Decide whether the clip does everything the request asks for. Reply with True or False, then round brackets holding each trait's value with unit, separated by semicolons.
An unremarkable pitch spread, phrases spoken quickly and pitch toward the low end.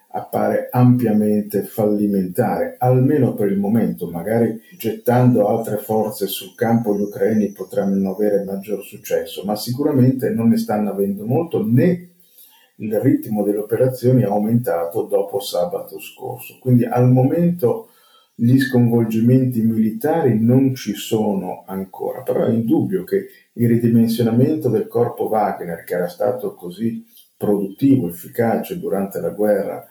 False (3.9 semitones; 130 wpm; 115 Hz)